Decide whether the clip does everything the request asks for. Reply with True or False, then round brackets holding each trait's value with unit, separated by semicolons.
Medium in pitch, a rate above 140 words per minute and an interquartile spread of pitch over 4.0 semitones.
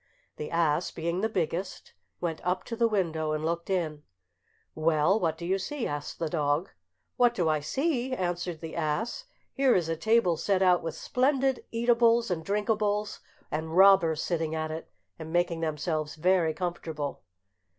True (175 Hz; 165 wpm; 4.6 semitones)